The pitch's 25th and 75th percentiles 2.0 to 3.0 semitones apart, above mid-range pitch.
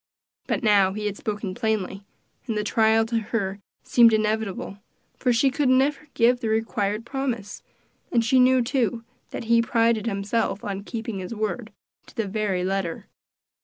Yes: narrow, 2.6 semitones; high, 220 Hz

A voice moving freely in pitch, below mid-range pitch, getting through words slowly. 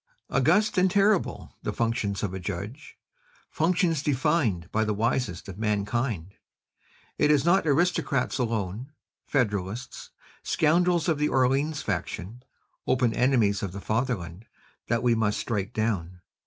Yes: wide, 6.5 semitones; low, 120 Hz; slow, 130 wpm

